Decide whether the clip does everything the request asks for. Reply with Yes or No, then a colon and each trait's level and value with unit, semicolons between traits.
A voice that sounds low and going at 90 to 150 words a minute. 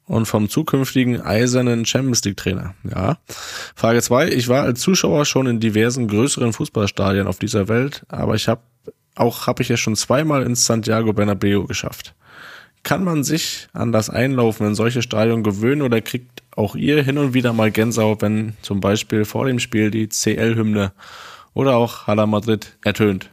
No: low, 115 Hz; average, 175 wpm